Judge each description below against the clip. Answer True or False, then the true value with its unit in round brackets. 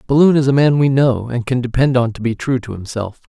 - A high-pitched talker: False (125 Hz)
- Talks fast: True (270 wpm)